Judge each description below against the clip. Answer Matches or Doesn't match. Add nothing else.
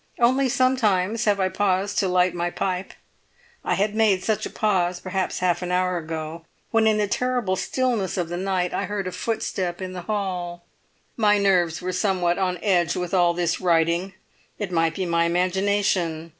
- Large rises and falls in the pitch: Doesn't match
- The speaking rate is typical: Matches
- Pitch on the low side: Doesn't match